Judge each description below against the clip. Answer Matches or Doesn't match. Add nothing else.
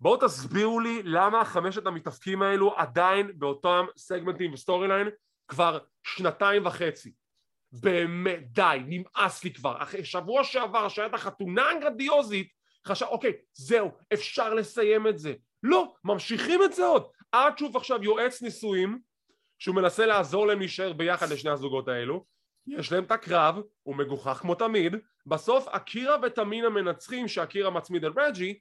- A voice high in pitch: Matches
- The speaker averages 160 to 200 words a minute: Doesn't match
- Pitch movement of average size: Matches